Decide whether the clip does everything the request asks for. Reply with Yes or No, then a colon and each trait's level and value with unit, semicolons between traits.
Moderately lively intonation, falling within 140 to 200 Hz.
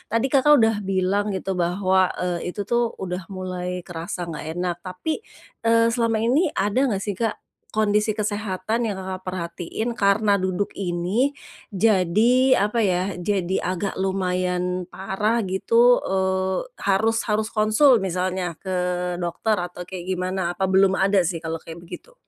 Yes: average, 3.2 semitones; high, 190 Hz